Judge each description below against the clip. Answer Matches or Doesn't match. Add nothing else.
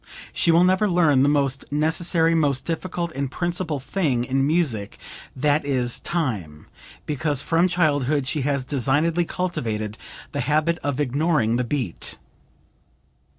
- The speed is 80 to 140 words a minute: Matches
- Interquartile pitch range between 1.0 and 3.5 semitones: Doesn't match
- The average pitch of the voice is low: Doesn't match